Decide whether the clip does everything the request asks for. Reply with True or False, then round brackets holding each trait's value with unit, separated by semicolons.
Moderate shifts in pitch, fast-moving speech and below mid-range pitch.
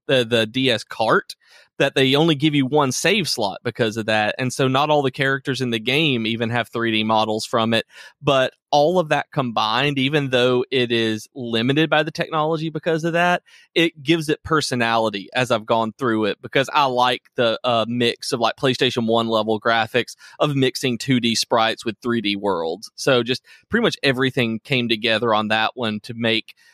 False (4.1 semitones; 195 wpm; 125 Hz)